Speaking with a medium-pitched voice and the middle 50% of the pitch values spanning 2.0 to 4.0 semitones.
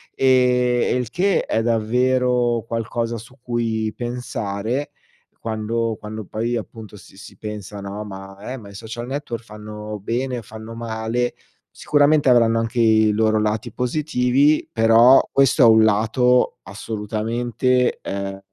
No: low, 115 Hz; narrow, 2.5 semitones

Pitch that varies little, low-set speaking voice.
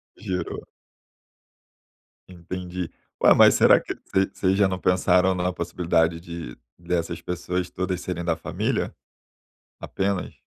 Yes: narrow, 1.4 semitones; very low, 90 Hz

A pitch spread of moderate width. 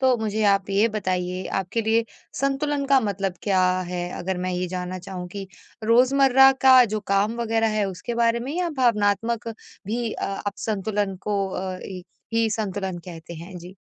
Yes: average, 3.8 semitones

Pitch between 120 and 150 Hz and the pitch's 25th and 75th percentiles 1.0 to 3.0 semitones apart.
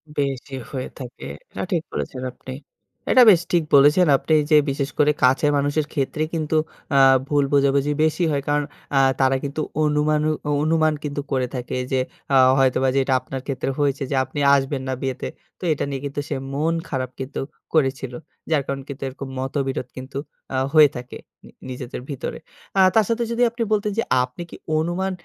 Yes: medium, 140 Hz; narrow, 2.5 semitones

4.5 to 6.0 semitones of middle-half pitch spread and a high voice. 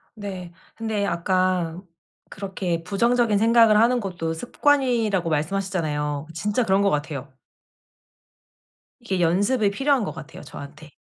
Yes: average, 5.2 semitones; high, 195 Hz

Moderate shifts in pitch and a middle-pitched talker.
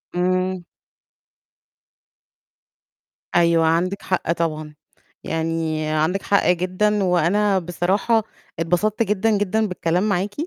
Yes: average, 3.3 semitones; medium, 180 Hz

